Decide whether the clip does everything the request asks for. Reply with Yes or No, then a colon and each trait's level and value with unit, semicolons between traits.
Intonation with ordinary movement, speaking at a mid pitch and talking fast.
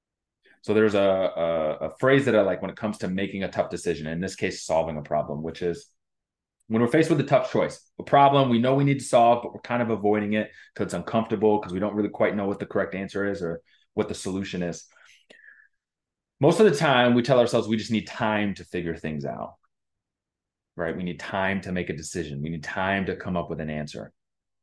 No: average, 4.6 semitones; low, 100 Hz; fast, 235 wpm